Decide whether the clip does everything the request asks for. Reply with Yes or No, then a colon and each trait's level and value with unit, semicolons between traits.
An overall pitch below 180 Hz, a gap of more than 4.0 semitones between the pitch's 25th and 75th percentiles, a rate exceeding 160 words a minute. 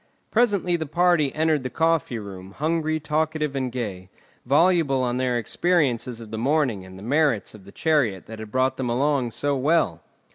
Yes: low, 135 Hz; average, 5.3 semitones; average, 180 wpm